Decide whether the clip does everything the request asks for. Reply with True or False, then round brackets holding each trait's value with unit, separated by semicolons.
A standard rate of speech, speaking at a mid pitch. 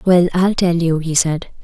False (220 wpm; 170 Hz)